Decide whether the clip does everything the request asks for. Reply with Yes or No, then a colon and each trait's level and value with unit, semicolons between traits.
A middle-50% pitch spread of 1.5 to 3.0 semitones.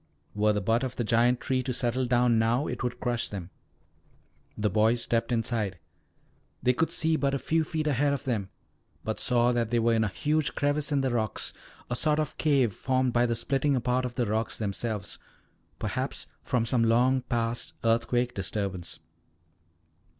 Yes: narrow, 2.5 semitones